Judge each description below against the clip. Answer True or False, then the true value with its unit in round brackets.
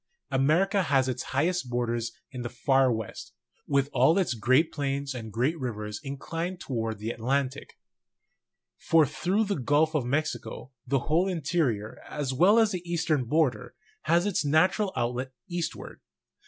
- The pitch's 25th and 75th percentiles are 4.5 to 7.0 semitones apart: True (5.1 semitones)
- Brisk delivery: False (150 wpm)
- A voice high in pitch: False (140 Hz)